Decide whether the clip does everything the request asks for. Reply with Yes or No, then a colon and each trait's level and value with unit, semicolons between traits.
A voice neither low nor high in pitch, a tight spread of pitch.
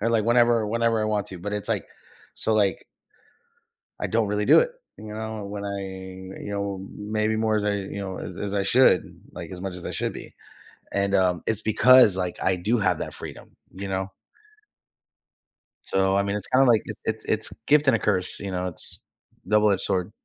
No: low, 100 Hz; narrow, 2.3 semitones